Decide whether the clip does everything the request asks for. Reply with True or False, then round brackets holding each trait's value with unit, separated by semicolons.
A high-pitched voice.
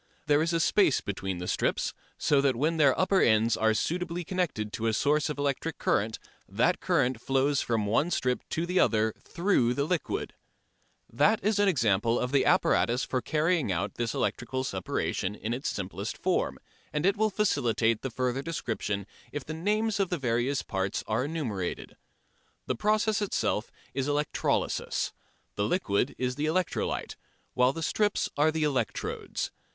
False (135 Hz)